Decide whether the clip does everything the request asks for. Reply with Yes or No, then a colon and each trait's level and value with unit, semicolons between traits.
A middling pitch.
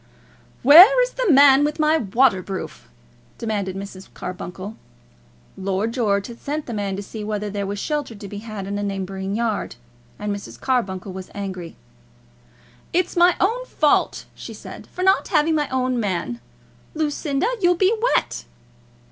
No: high, 215 Hz